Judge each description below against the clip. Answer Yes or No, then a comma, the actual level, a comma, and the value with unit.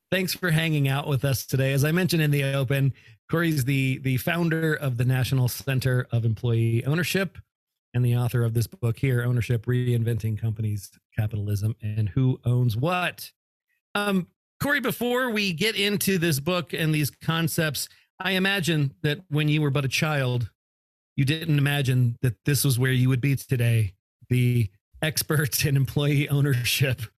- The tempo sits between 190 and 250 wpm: No, average, 165 wpm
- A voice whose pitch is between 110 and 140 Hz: Yes, low, 135 Hz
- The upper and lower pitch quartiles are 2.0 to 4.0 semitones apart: No, average, 4.7 semitones